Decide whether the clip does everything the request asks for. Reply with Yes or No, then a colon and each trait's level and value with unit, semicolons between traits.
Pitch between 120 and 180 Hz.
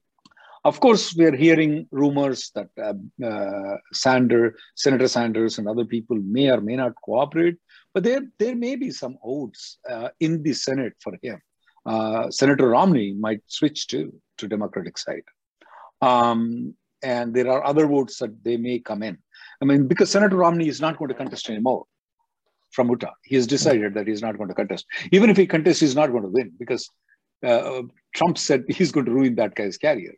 Yes: medium, 140 Hz